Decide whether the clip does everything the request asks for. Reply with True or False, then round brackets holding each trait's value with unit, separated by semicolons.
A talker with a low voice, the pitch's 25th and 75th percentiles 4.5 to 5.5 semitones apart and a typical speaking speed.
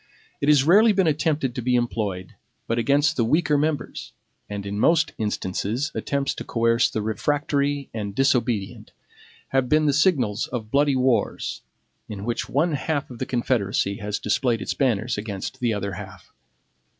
True (125 Hz; 5.2 semitones; 160 wpm)